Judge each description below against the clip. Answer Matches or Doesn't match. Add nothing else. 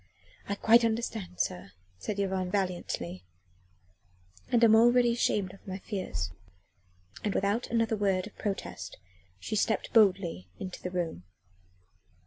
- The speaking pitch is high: Matches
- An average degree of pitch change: Matches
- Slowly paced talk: Matches